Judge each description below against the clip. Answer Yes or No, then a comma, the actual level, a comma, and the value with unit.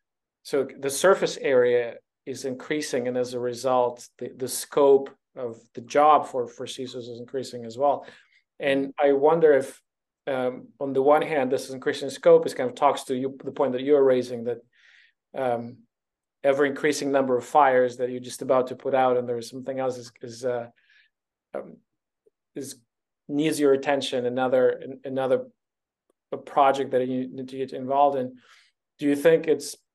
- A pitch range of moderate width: No, narrow, 2.3 semitones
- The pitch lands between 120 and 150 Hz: Yes, low, 135 Hz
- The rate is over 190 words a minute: No, average, 175 wpm